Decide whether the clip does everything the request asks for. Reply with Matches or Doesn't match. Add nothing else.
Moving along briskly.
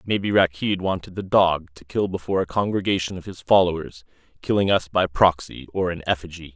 Doesn't match